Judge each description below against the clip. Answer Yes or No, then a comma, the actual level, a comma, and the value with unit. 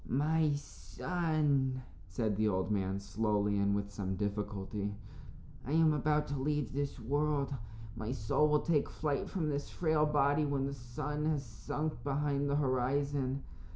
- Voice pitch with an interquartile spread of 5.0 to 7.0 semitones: Yes, wide, 5.5 semitones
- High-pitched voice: No, medium, 140 Hz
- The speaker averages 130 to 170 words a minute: Yes, average, 155 wpm